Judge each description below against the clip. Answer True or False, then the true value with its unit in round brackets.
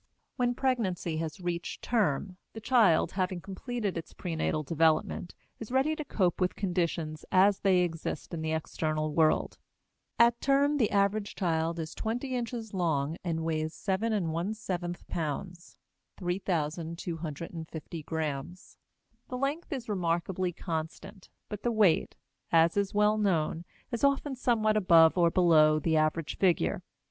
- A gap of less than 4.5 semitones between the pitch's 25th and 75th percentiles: False (4.8 semitones)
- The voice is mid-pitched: True (180 Hz)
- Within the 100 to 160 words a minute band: True (135 wpm)